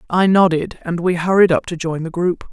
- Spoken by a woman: Yes, female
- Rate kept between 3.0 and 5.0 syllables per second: No, 5.3 syllables/s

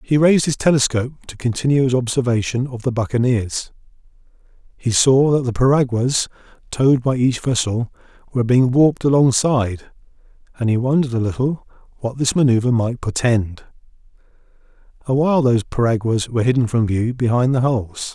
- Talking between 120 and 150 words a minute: Yes, average, 145 wpm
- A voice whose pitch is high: No, low, 125 Hz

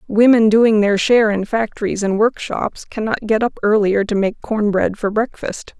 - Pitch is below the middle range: No, high, 215 Hz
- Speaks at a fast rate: No, average, 185 wpm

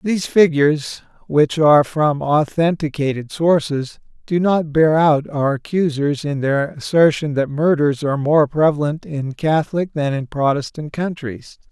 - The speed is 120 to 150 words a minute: Yes, average, 140 wpm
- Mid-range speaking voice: Yes, medium, 150 Hz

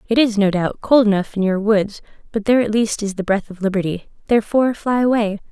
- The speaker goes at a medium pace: No, fast, 230 wpm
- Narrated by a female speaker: Yes, female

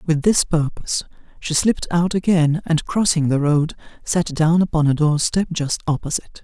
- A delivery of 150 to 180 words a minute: Yes, average, 175 wpm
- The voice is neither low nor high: Yes, medium, 160 Hz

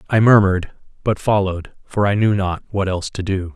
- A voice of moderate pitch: No, very low, 95 Hz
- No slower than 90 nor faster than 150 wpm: No, average, 200 wpm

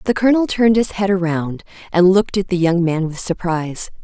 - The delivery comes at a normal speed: No, fast, 210 wpm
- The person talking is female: Yes, female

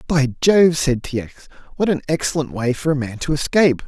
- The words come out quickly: Yes, fast, 215 wpm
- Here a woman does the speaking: No, male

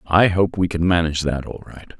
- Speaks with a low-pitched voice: Yes, very low, 85 Hz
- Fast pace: Yes, fast, 240 wpm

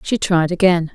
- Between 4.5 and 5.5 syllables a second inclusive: Yes, 4.7 syllables/s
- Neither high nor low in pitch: Yes, medium, 175 Hz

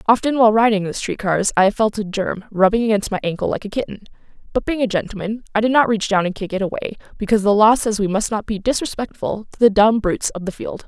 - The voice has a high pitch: Yes, high, 210 Hz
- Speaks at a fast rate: Yes, fast, 265 wpm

